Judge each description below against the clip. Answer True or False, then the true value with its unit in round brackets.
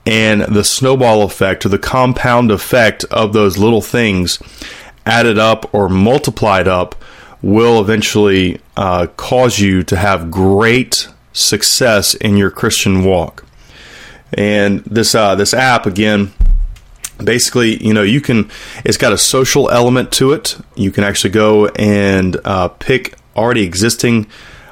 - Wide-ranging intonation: False (2.9 semitones)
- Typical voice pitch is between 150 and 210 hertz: False (105 Hz)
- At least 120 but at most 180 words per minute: True (140 wpm)